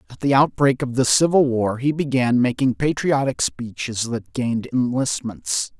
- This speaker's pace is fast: No, average, 155 wpm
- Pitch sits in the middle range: No, low, 130 Hz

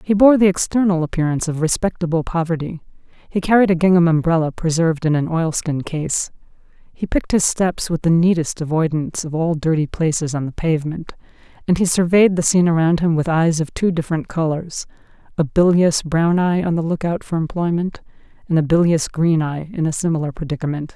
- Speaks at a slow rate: No, average, 180 wpm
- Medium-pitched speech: Yes, medium, 165 Hz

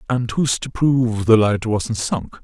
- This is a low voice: Yes, low, 115 Hz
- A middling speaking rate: Yes, average, 195 wpm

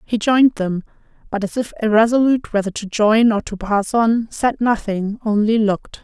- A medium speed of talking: Yes, average, 180 wpm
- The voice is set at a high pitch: Yes, high, 220 Hz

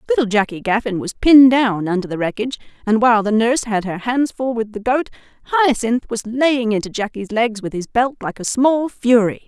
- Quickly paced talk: Yes, fast, 210 wpm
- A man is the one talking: No, female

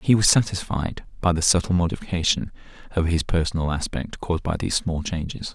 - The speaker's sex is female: No, male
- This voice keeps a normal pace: Yes, average, 175 wpm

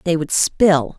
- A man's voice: No, female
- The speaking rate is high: No, average, 185 wpm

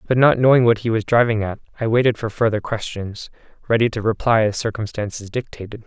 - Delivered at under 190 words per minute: No, average, 195 wpm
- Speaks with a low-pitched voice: Yes, low, 110 Hz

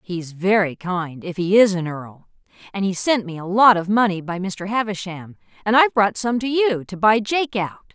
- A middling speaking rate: No, fast, 220 wpm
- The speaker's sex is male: No, female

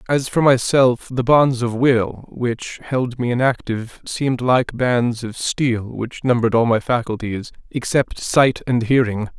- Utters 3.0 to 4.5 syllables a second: Yes, 4.0 syllables/s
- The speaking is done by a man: Yes, male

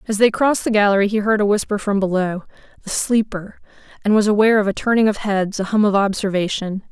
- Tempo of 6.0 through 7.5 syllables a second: Yes, 6.3 syllables/s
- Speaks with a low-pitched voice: No, high, 205 Hz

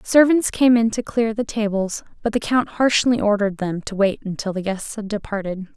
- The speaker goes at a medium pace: No, fast, 210 wpm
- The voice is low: No, high, 215 Hz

